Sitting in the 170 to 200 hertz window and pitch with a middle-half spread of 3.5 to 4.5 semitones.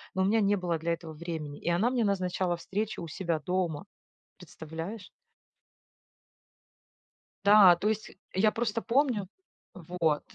Yes: medium, 185 Hz; average, 3.9 semitones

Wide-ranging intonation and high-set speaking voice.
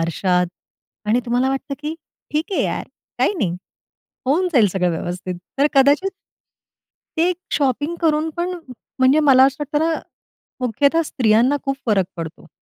Yes: wide, 6.0 semitones; very high, 270 Hz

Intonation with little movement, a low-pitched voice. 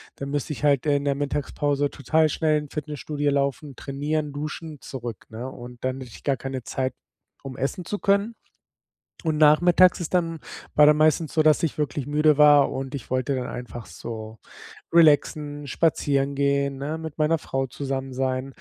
No: narrow, 2.3 semitones; medium, 145 Hz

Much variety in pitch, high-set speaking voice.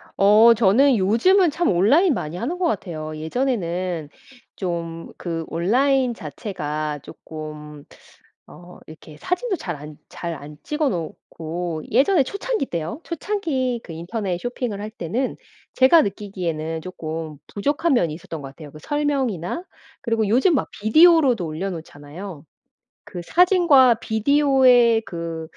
Yes: wide, 8.5 semitones; high, 200 Hz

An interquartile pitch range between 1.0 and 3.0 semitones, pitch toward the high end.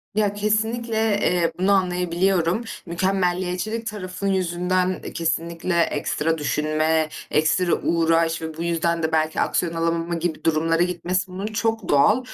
No: average, 2.7 semitones; medium, 175 Hz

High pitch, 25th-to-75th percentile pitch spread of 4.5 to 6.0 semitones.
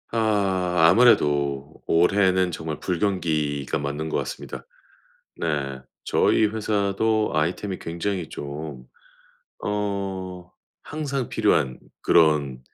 No: very low, 90 Hz; average, 5.3 semitones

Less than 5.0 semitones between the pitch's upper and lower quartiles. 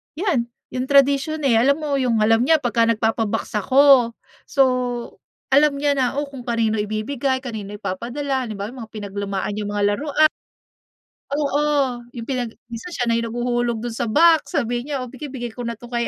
Yes: average, 3.7 semitones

